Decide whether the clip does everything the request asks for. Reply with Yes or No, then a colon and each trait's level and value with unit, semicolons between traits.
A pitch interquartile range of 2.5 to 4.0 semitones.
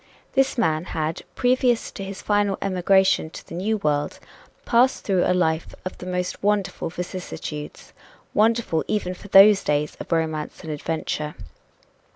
No: average, 4.4 semitones